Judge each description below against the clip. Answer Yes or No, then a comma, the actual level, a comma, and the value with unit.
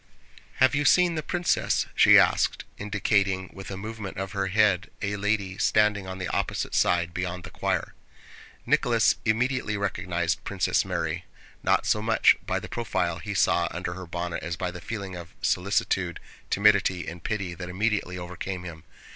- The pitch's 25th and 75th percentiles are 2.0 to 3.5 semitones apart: Yes, average, 3.0 semitones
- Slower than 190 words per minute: Yes, average, 165 wpm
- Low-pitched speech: Yes, very low, 95 Hz